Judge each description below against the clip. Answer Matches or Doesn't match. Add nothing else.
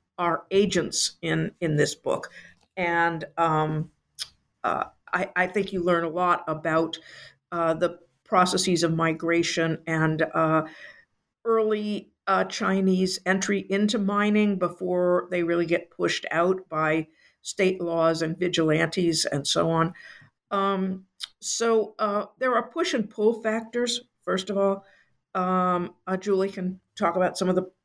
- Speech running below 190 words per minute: Matches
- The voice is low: Doesn't match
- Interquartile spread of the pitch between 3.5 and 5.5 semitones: Doesn't match